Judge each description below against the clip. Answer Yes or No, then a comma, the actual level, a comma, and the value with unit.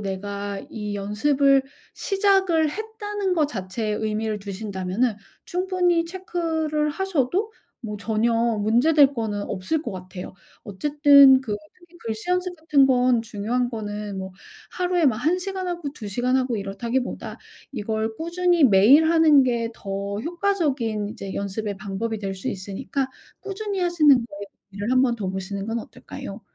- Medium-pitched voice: No, high, 245 Hz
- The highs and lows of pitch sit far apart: Yes, wide, 7.6 semitones